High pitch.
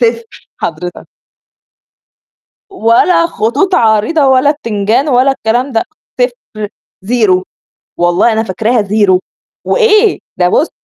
Yes: high, 230 Hz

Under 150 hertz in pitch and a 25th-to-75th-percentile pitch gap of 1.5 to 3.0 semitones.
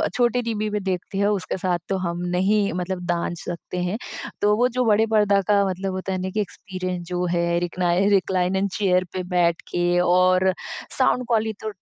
No: high, 190 Hz; average, 2.7 semitones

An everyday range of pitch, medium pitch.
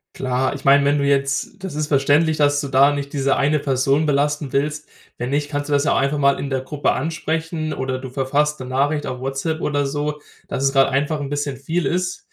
No: narrow, 1.6 semitones; medium, 145 Hz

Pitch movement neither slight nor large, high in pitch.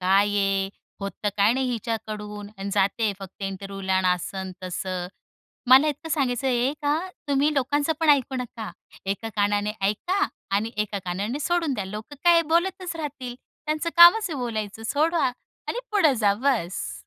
No: wide, 6.6 semitones; high, 230 Hz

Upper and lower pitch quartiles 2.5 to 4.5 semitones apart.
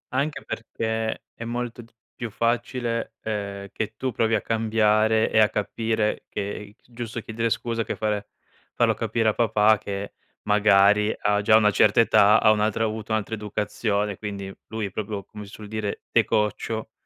No: narrow, 1.5 semitones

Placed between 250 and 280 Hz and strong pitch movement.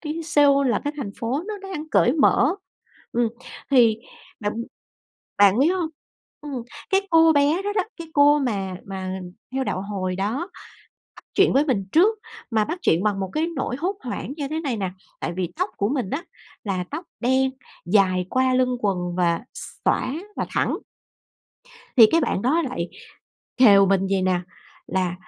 Yes: very high, 255 Hz; wide, 7.6 semitones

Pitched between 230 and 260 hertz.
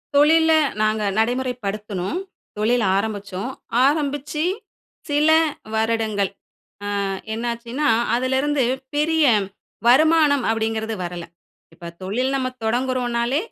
Yes: high, 245 Hz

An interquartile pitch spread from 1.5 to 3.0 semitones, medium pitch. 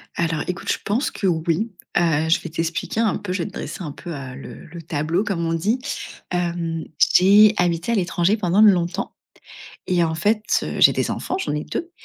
No: average, 3.5 semitones; medium, 175 Hz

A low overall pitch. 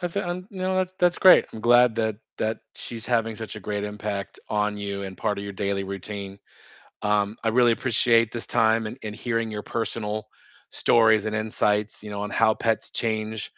Yes: low, 110 Hz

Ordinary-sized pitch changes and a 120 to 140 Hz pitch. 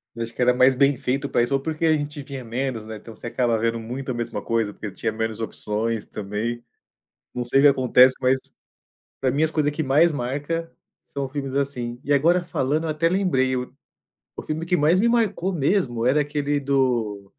Yes: average, 3.9 semitones; low, 135 Hz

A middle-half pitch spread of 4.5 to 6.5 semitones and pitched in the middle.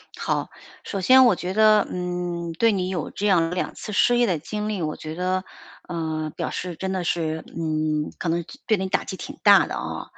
No: average, 3.6 semitones; medium, 180 Hz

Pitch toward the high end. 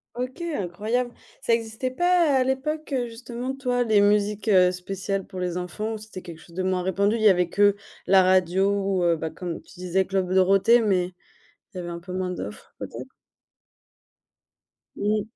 Yes: high, 195 Hz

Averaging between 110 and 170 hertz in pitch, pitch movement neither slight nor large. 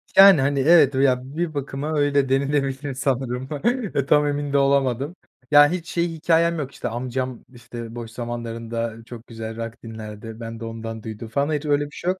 Yes: low, 135 Hz; average, 4.0 semitones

